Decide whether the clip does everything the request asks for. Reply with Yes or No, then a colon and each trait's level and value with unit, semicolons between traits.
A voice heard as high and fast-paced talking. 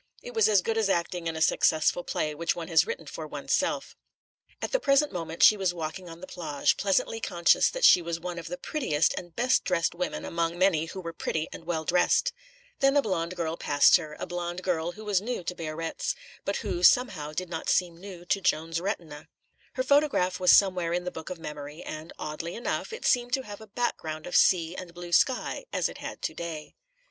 No: medium, 175 Hz; fast, 220 wpm